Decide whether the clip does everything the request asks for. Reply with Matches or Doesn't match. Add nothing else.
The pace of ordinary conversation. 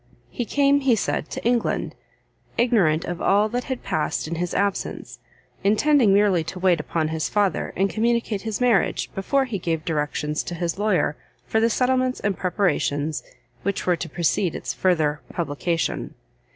Matches